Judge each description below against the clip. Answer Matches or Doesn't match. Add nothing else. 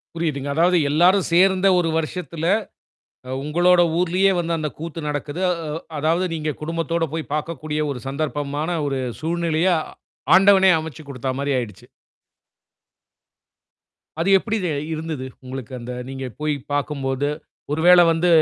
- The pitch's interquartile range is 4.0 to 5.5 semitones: Doesn't match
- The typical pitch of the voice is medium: Matches